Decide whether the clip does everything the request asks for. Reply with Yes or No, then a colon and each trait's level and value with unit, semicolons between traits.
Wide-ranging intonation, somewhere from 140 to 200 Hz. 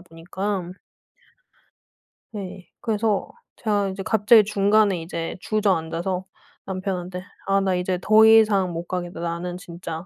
No: average, 2.8 semitones; high, 190 Hz